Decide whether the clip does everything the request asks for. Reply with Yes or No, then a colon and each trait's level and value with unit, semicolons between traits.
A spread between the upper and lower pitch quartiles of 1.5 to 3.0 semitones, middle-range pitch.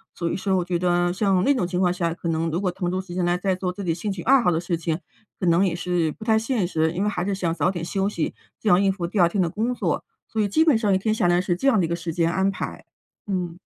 Yes: narrow, 2.5 semitones; medium, 180 Hz